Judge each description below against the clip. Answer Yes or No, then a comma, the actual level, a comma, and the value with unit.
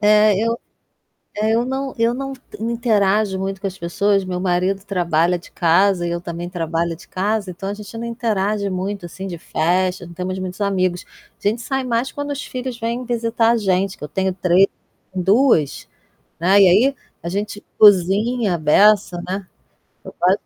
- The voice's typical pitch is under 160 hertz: No, high, 195 Hz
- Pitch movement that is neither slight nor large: Yes, average, 3.8 semitones